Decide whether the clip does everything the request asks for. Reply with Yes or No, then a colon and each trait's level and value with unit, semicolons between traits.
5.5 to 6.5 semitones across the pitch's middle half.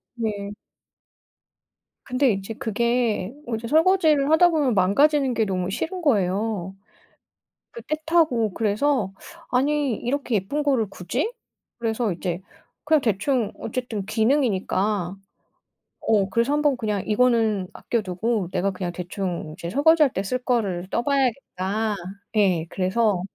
Yes: wide, 5.9 semitones